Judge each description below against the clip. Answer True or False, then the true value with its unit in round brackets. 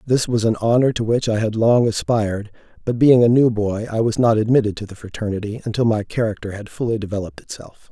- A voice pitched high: False (110 Hz)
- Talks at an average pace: False (220 wpm)